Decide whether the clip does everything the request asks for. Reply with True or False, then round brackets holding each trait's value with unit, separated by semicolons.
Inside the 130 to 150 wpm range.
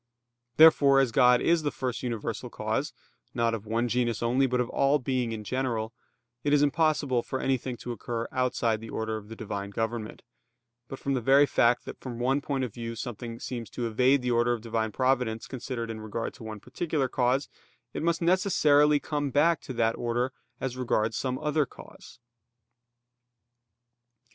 False (180 wpm)